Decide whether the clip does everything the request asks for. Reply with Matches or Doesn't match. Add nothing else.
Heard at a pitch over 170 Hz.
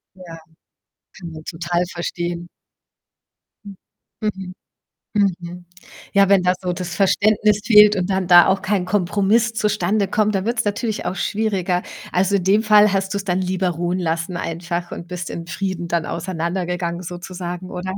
Matches